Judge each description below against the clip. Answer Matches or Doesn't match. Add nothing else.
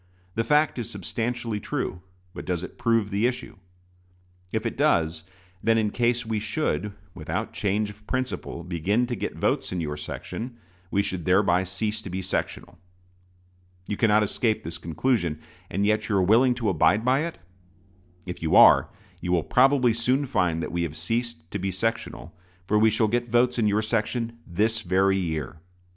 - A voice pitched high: Doesn't match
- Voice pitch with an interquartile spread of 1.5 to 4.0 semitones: Doesn't match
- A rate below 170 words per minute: Doesn't match